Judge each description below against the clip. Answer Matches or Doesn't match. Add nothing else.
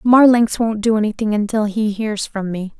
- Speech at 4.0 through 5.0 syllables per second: Matches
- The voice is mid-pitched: Doesn't match